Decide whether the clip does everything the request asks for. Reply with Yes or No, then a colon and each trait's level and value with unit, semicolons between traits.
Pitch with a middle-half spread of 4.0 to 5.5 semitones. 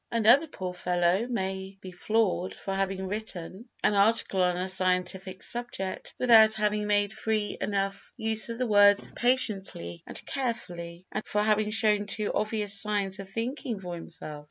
No: average, 2.8 semitones